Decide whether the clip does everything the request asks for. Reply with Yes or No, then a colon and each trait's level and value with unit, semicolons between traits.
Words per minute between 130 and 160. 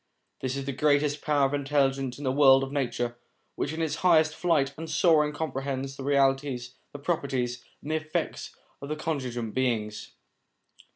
No: average, 170 wpm